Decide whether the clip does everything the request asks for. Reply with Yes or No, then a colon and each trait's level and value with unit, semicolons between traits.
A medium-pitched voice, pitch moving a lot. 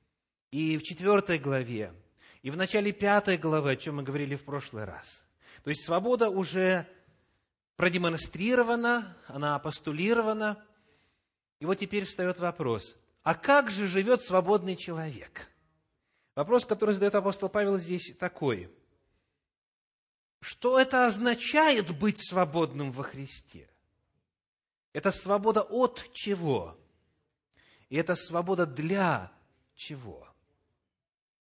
Yes: medium, 180 Hz; wide, 6.4 semitones